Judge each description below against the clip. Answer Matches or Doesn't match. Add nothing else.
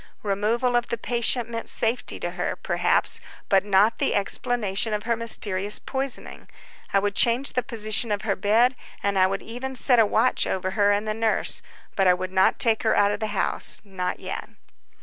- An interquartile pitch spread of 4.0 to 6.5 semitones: Doesn't match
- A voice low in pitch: Doesn't match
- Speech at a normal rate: Matches